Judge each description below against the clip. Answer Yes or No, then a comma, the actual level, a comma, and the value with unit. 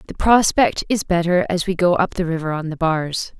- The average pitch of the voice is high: No, medium, 175 Hz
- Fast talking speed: Yes, fast, 230 wpm